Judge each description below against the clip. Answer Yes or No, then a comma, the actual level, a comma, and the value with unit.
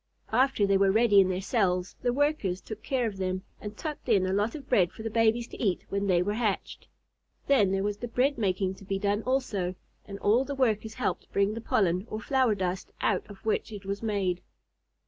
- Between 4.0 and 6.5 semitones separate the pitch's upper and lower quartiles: No, average, 3.2 semitones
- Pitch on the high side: Yes, high, 205 Hz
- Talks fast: Yes, fast, 225 wpm